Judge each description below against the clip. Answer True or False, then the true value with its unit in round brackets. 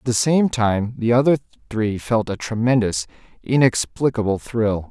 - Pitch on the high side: False (115 Hz)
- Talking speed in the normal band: True (145 wpm)